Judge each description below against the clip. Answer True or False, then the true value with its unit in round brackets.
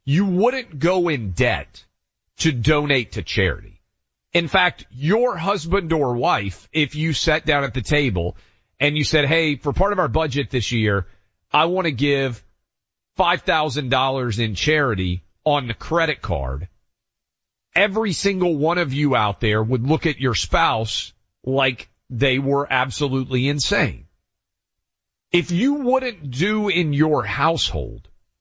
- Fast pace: False (145 wpm)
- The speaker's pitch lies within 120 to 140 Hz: True (135 Hz)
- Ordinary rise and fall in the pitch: False (7.7 semitones)